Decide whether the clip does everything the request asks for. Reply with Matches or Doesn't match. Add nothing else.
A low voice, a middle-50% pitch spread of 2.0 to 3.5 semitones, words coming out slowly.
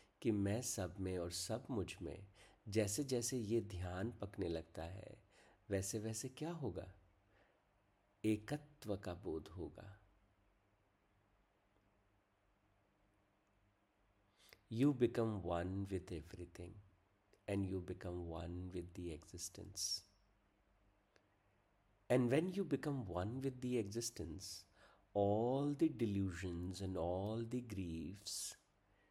Matches